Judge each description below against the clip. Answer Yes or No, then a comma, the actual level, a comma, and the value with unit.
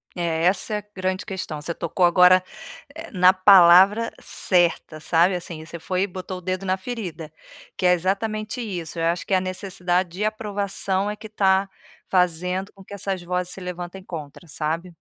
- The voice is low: No, medium, 185 Hz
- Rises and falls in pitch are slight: Yes, narrow, 2.0 semitones